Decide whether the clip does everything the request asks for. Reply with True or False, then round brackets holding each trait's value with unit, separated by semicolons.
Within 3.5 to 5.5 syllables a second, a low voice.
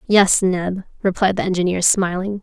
False (4.7 syllables/s; 190 Hz)